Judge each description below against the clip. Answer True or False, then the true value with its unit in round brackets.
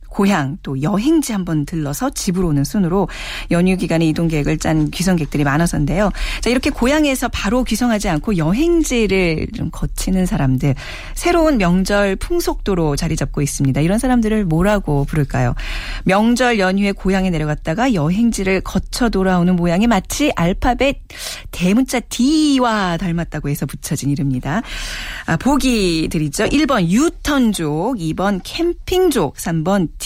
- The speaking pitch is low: False (190 Hz)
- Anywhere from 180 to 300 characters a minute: False (325 characters per minute)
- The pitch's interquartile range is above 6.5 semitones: True (7.1 semitones)